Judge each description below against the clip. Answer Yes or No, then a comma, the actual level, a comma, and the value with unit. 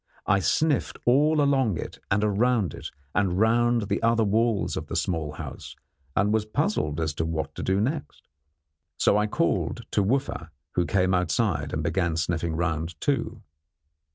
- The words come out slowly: No, average, 165 wpm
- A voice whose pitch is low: Yes, low, 100 Hz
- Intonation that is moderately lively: No, wide, 5.8 semitones